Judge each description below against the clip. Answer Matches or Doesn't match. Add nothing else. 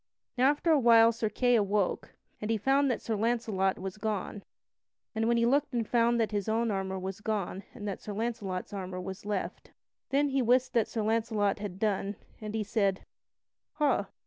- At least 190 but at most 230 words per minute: Matches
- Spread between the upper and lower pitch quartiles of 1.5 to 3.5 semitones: Matches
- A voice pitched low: Doesn't match